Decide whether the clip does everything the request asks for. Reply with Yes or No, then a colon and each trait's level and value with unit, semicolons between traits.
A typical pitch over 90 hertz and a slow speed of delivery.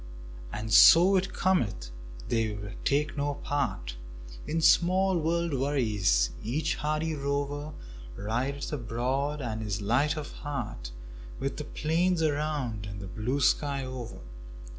Yes: medium, 140 Hz; slow, 125 wpm